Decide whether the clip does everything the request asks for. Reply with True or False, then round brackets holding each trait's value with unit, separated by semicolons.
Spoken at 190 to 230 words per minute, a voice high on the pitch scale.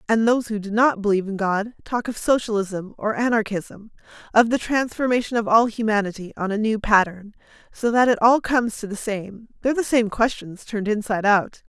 True (195 wpm; 220 Hz)